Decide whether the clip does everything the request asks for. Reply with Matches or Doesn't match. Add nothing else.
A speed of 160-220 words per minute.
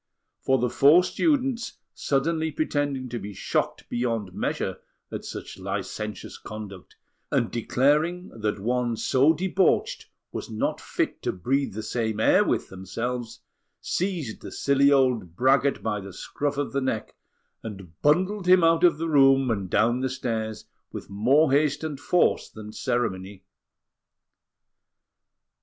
Doesn't match